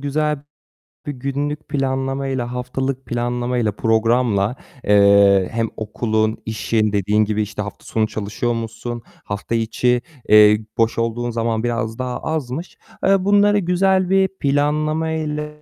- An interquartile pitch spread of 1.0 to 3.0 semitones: No, average, 4.8 semitones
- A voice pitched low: Yes, low, 120 Hz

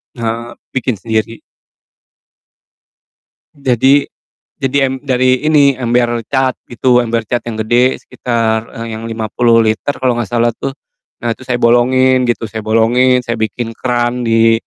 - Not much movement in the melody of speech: Yes, narrow, 2.1 semitones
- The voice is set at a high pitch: No, low, 120 Hz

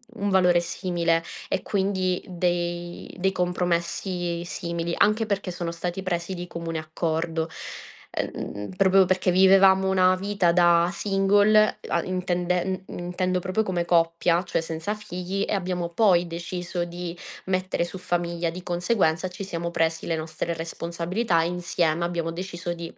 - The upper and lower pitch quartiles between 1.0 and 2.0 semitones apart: Yes, narrow, 1.7 semitones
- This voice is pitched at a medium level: Yes, medium, 175 Hz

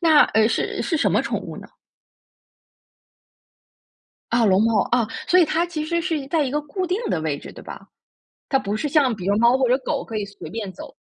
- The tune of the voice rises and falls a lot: Yes, wide, 6.7 semitones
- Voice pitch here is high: Yes, very high, 255 Hz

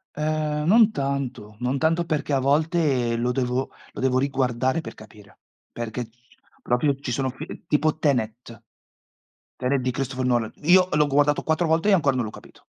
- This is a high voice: No, low, 135 Hz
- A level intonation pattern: No, average, 3.8 semitones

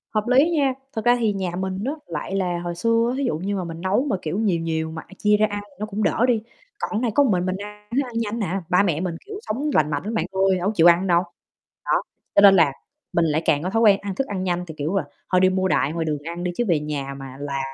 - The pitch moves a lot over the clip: No, average, 4.1 semitones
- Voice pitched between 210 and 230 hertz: No, high, 190 Hz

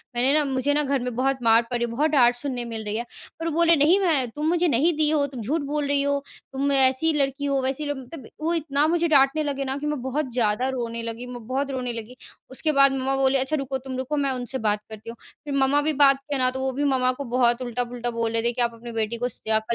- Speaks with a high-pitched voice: Yes, very high, 265 Hz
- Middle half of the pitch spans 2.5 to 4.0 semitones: Yes, average, 2.9 semitones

